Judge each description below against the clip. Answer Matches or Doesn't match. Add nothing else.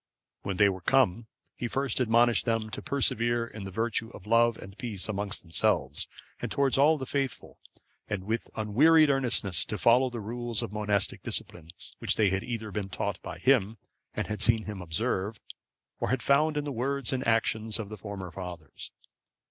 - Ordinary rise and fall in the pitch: Matches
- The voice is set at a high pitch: Doesn't match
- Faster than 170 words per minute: Matches